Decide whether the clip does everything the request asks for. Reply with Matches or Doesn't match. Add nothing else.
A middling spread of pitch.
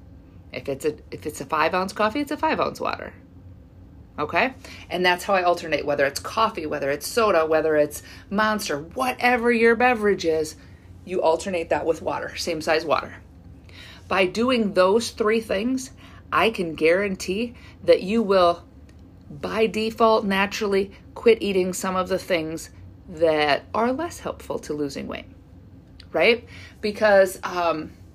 Doesn't match